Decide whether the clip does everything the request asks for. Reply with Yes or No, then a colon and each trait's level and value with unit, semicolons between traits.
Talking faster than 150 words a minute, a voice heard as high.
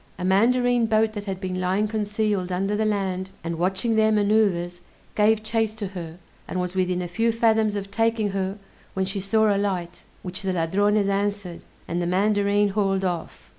Yes: average, 185 wpm; high, 200 Hz